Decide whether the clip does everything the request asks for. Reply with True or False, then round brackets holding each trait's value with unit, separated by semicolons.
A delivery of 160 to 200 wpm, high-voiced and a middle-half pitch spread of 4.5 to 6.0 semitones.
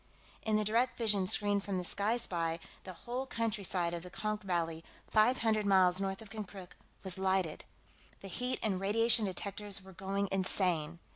False (170 wpm; 195 Hz; 2.7 semitones)